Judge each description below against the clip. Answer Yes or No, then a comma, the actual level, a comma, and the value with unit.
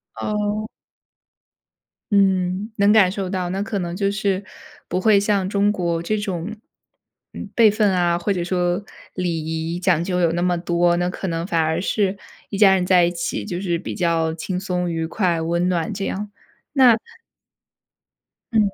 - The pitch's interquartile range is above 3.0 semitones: No, average, 2.7 semitones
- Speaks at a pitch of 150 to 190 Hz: Yes, medium, 185 Hz